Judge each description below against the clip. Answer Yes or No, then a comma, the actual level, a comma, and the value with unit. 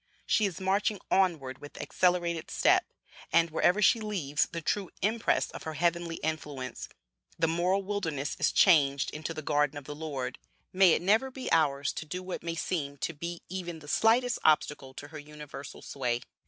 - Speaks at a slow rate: No, average, 180 wpm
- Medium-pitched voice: Yes, medium, 165 Hz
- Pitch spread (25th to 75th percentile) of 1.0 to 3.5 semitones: No, average, 4.2 semitones